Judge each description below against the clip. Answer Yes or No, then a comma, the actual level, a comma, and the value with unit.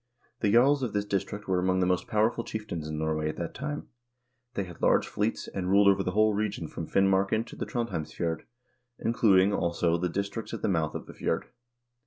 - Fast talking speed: Yes, fast, 210 wpm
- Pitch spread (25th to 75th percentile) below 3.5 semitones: No, average, 3.8 semitones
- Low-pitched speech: Yes, very low, 95 Hz